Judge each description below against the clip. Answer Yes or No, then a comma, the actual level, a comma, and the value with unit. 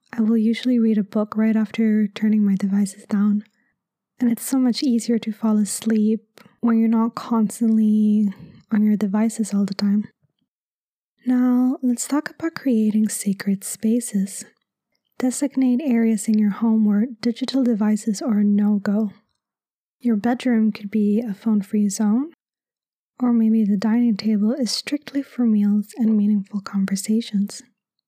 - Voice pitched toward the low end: No, high, 220 Hz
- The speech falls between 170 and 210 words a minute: No, average, 145 wpm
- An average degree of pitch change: No, narrow, 2.1 semitones